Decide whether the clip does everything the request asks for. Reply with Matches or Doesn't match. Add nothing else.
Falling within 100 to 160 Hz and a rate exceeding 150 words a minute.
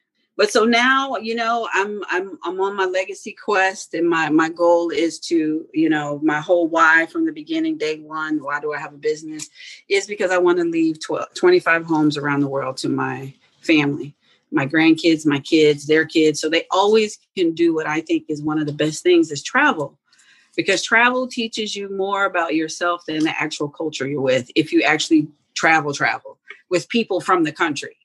Doesn't match